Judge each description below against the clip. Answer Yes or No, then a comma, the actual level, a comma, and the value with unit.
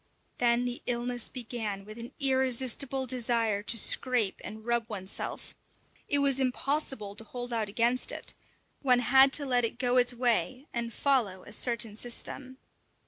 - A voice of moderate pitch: No, high, 245 Hz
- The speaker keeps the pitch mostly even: Yes, narrow, 2.3 semitones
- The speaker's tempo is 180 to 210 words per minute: No, average, 155 wpm